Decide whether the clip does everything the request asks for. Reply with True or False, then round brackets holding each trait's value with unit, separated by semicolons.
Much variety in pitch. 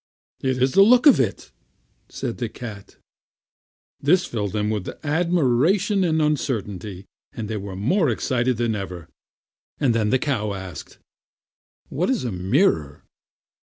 True (7.5 semitones)